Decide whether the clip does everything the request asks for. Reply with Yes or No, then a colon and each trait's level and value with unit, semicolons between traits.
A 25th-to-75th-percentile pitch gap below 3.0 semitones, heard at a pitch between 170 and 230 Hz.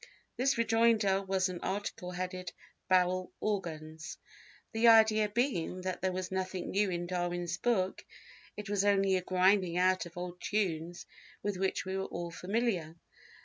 Yes: narrow, 2.4 semitones; medium, 185 Hz